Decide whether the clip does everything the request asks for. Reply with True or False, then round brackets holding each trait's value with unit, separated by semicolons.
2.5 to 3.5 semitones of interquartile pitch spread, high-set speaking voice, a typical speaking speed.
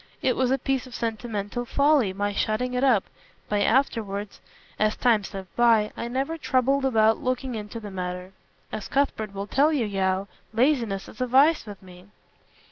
False (4.2 semitones; 225 Hz; 175 wpm)